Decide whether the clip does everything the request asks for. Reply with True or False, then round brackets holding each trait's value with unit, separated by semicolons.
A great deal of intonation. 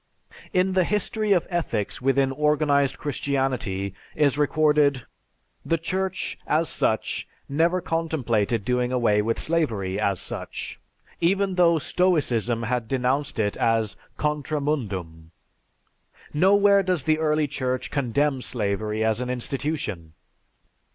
True (5.8 semitones)